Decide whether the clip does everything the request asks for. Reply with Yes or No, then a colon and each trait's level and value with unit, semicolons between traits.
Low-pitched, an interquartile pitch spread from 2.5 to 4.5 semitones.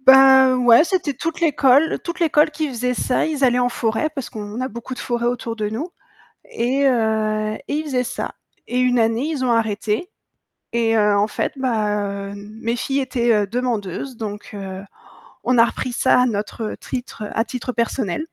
No: high, 240 Hz; average, 3.5 semitones